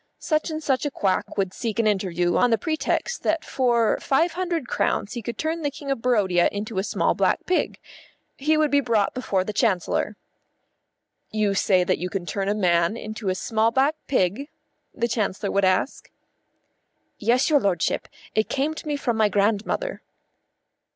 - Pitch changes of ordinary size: No, wide, 6.1 semitones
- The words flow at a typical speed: Yes, average, 180 wpm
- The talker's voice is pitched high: Yes, high, 225 Hz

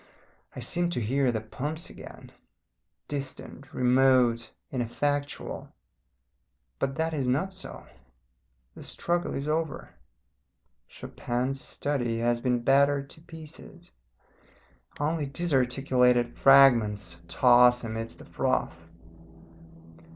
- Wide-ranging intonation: No, average, 3.2 semitones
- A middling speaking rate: No, slow, 100 wpm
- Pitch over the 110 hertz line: Yes, low, 135 Hz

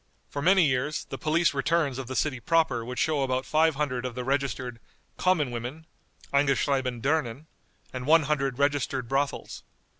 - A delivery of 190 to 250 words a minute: No, average, 160 wpm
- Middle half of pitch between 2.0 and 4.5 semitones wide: Yes, average, 3.2 semitones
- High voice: No, medium, 140 Hz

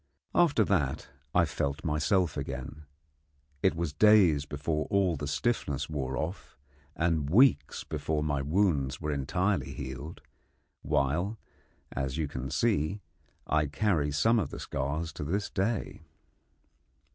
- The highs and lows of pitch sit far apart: No, average, 5.0 semitones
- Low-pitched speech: Yes, very low, 75 Hz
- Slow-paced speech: Yes, slow, 130 wpm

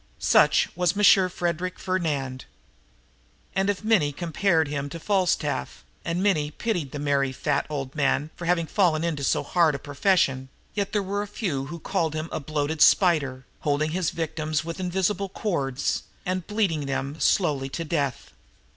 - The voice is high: No, medium, 160 Hz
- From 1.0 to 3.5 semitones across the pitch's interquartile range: No, average, 4.4 semitones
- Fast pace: No, average, 165 wpm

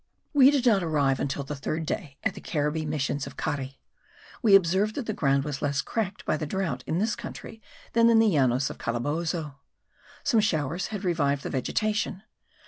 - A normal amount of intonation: No, wide, 6.8 semitones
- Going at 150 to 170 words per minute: No, average, 190 wpm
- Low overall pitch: No, medium, 160 Hz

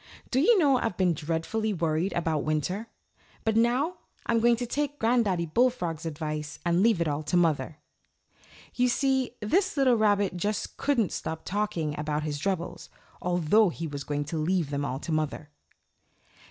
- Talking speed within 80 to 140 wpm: No, average, 165 wpm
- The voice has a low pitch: No, medium, 180 Hz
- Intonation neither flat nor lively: No, wide, 6.8 semitones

